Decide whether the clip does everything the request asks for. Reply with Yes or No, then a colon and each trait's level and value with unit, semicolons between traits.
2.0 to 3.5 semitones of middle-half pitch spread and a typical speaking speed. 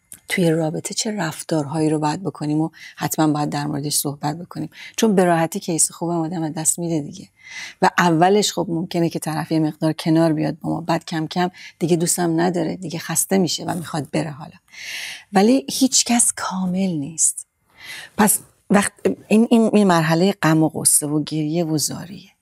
No: average, 2.8 semitones; fast, 175 wpm